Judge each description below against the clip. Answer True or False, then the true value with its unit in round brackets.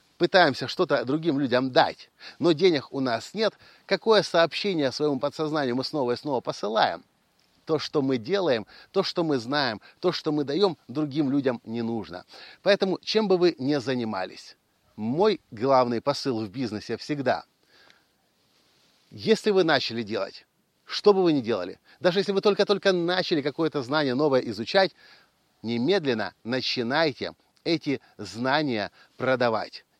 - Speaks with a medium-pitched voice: True (150 Hz)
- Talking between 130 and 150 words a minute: True (140 wpm)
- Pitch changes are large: True (6.1 semitones)